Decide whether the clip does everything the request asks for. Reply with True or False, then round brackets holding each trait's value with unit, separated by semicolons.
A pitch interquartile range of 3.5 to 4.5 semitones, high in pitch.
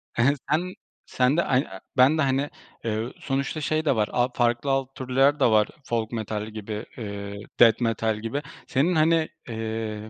False (4.2 semitones; 125 Hz)